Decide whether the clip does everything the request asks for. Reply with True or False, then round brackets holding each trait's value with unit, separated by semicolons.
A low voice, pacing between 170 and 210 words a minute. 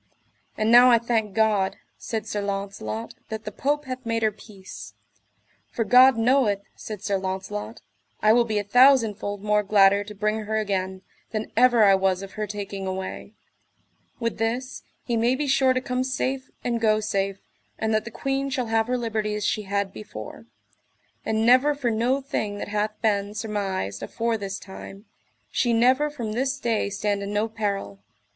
False (215 Hz; 180 wpm)